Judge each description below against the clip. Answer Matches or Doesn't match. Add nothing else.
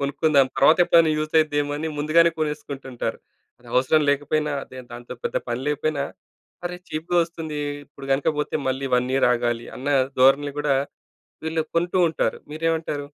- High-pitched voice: Doesn't match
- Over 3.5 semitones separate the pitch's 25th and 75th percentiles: Doesn't match